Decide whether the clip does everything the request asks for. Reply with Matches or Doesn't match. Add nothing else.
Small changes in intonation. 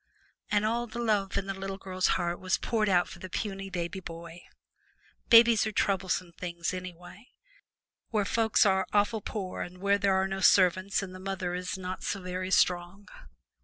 Matches